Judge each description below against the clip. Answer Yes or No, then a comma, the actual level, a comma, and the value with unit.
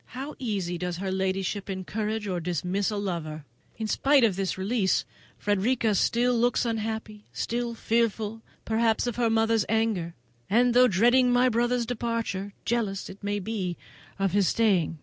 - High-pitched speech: Yes, high, 215 Hz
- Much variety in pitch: No, average, 3.5 semitones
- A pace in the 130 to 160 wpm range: Yes, average, 155 wpm